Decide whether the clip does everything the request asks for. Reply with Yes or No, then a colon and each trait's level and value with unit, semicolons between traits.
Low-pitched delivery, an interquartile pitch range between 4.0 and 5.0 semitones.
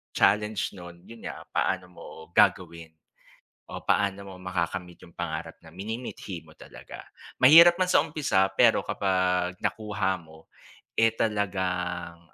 No: very low, 95 Hz; average, 3.3 semitones